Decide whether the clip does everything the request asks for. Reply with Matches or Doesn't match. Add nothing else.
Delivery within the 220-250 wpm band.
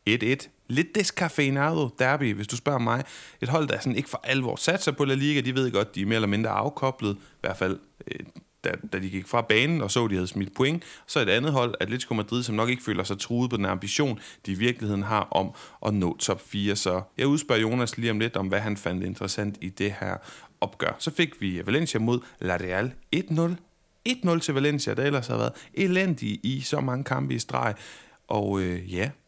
Matches